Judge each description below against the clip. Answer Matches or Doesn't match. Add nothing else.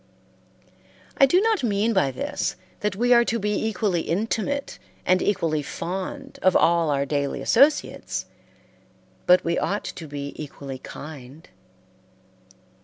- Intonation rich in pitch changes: Matches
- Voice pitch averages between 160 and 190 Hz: Matches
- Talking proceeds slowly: Matches